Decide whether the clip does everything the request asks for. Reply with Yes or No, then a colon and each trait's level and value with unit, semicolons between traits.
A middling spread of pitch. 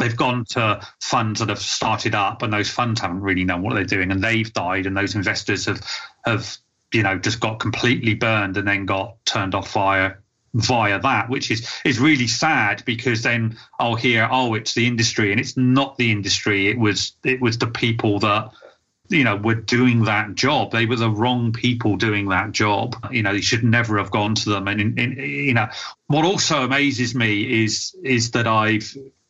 Yes: average, 3.1 semitones